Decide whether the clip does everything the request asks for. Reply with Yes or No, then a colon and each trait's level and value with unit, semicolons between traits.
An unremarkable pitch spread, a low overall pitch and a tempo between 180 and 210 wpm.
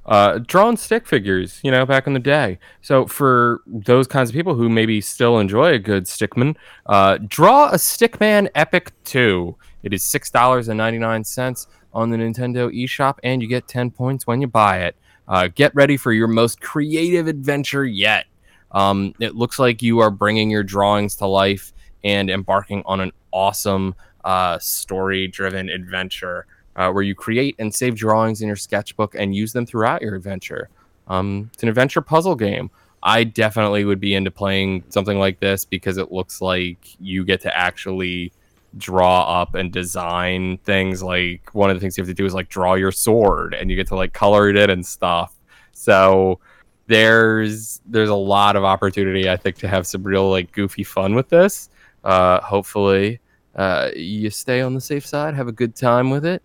Yes: average, 4.4 semitones; low, 100 Hz; average, 190 wpm